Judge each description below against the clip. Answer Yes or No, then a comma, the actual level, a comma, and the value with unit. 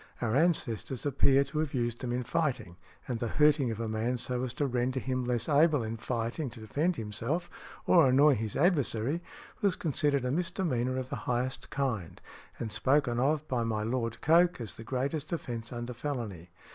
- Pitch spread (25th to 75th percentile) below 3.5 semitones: No, average, 3.9 semitones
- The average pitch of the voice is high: No, low, 130 Hz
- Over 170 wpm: Yes, average, 185 wpm